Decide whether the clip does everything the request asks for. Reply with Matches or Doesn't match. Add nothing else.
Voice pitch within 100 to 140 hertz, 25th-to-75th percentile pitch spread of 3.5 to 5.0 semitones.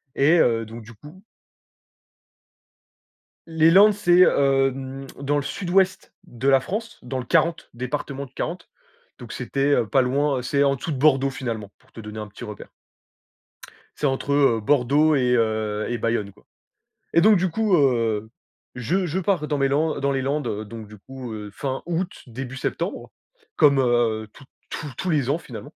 Matches